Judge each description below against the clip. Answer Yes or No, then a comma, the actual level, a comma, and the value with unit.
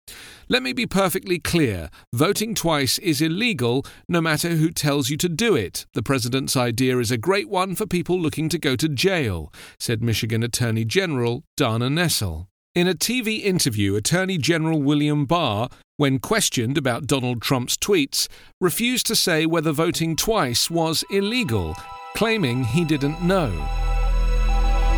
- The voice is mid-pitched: Yes, medium, 160 Hz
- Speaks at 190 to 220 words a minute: No, average, 150 wpm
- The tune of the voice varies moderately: No, wide, 6.3 semitones